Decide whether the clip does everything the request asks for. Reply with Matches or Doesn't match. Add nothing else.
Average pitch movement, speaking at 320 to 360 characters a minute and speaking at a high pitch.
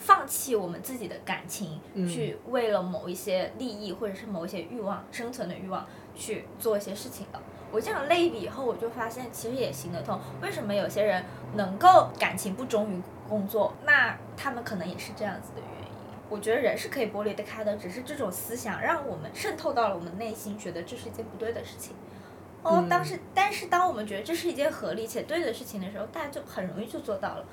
Matches